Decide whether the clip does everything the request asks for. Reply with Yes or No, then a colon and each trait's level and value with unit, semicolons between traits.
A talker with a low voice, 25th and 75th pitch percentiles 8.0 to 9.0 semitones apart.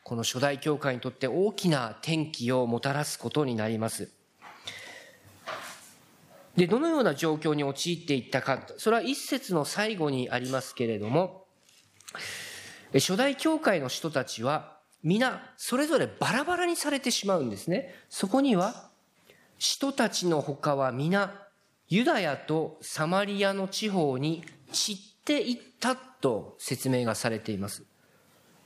No: medium, 165 Hz; wide, 8.6 semitones